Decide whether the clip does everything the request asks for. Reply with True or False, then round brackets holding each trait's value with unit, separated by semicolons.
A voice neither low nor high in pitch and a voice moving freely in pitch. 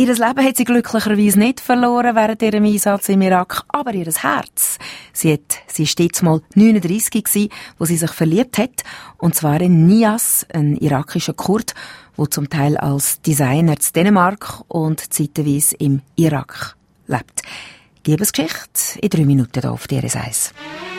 True (180 Hz; 6.3 semitones)